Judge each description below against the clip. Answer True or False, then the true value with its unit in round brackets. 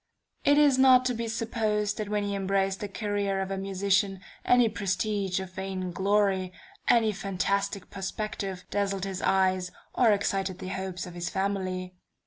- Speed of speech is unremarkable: True (160 wpm)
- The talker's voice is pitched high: True (195 Hz)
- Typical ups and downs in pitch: False (1.8 semitones)